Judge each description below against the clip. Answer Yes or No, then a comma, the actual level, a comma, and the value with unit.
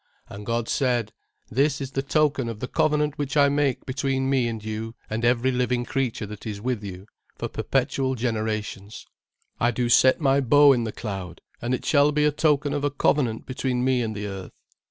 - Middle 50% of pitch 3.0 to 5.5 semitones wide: Yes, average, 3.8 semitones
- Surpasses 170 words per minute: Yes, average, 200 wpm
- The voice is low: Yes, low, 125 Hz